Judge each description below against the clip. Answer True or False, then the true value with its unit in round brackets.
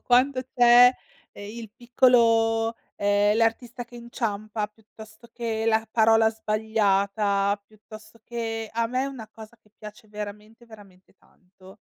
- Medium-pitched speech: False (220 Hz)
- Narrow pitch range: True (1.9 semitones)